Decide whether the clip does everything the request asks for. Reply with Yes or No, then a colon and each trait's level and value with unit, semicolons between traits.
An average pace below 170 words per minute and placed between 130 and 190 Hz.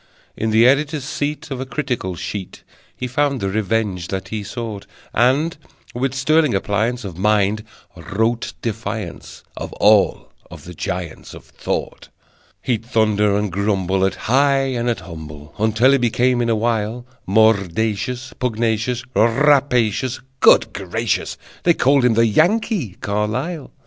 No: average, 140 wpm; low, 115 Hz